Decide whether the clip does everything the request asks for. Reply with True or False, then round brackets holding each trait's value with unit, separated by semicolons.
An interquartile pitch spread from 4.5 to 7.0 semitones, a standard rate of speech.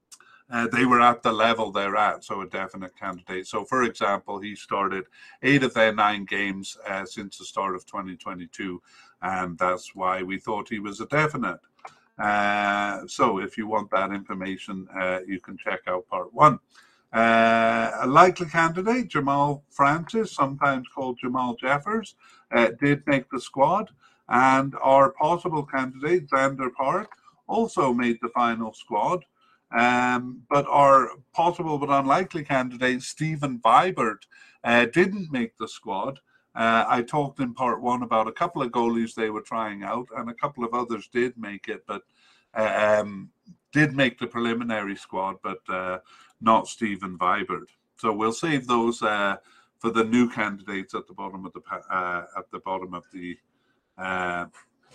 True (5.5 semitones; 160 wpm)